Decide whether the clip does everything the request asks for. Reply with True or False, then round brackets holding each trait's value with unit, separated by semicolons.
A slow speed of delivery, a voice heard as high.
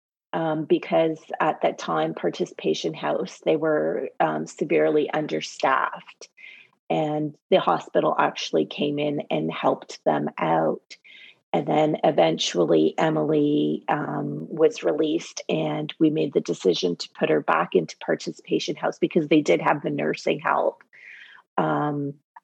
False (130 wpm; 150 Hz)